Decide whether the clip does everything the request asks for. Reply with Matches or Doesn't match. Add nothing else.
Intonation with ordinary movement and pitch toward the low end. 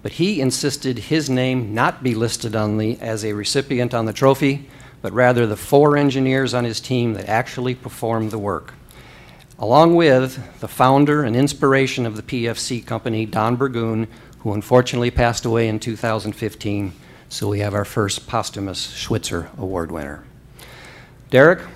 Matches